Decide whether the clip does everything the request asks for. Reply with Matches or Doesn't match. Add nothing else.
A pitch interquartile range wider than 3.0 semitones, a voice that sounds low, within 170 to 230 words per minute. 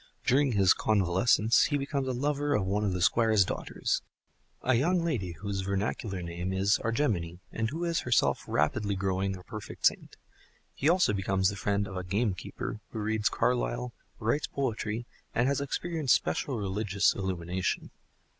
Doesn't match